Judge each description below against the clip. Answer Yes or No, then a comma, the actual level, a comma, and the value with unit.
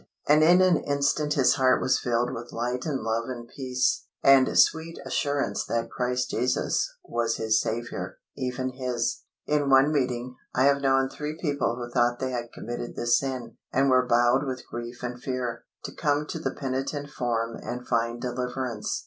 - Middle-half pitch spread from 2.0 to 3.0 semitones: Yes, narrow, 2.4 semitones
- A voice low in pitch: Yes, low, 125 Hz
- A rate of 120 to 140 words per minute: No, average, 175 wpm